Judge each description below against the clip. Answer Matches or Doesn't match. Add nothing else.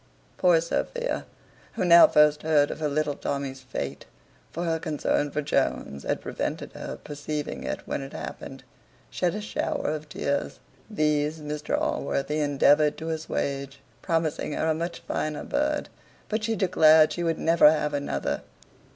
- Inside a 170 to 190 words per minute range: Doesn't match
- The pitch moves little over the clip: Matches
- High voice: Doesn't match